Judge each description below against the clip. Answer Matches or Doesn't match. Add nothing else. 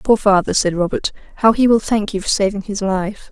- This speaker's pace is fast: Matches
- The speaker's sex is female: Matches